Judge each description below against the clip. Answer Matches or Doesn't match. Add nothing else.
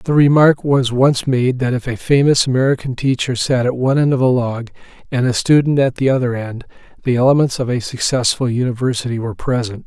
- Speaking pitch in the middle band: Doesn't match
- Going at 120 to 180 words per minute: Doesn't match